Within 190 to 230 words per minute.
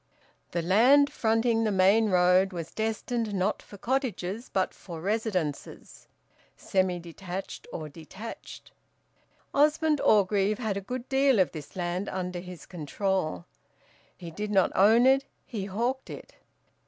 No: slow, 135 wpm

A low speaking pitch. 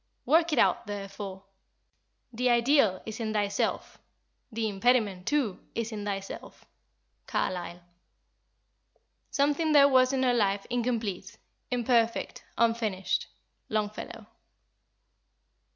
No: high, 225 Hz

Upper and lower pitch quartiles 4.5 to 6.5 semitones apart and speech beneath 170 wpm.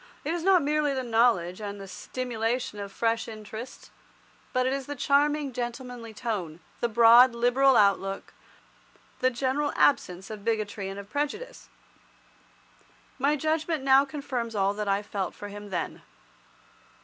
Yes: average, 5.0 semitones; average, 150 wpm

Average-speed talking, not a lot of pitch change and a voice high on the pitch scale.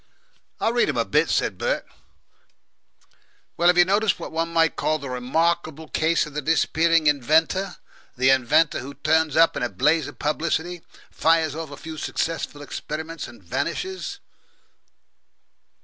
No: average, 150 wpm; narrow, 2.3 semitones; medium, 160 Hz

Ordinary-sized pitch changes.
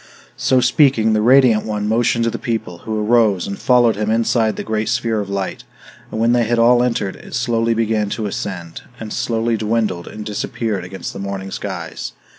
No: narrow, 2.0 semitones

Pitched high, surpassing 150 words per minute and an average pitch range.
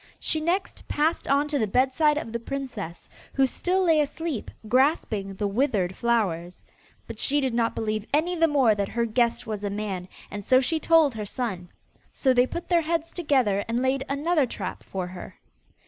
No: very high, 255 Hz; average, 190 wpm; wide, 6.1 semitones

